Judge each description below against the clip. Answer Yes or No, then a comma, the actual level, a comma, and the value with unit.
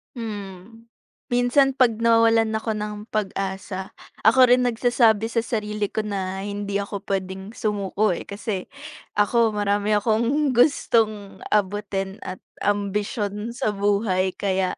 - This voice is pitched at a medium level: No, high, 210 Hz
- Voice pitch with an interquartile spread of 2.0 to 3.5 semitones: Yes, narrow, 2.4 semitones